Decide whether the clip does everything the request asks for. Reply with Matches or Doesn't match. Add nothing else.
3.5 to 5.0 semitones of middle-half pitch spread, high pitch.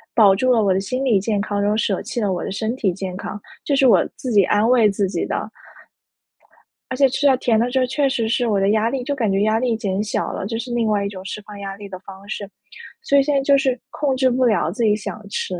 Matches